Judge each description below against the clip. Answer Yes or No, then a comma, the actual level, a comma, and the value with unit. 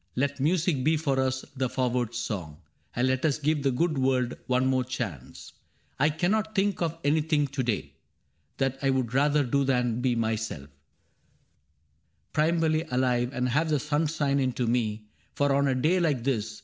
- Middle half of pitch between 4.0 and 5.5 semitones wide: No, average, 3.5 semitones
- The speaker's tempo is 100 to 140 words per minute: No, average, 175 wpm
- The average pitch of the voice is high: No, low, 135 Hz